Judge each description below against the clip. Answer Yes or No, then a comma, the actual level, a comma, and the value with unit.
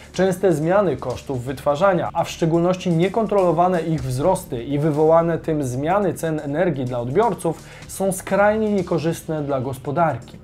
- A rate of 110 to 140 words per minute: Yes, average, 130 wpm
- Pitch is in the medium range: Yes, medium, 165 Hz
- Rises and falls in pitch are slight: No, average, 4.4 semitones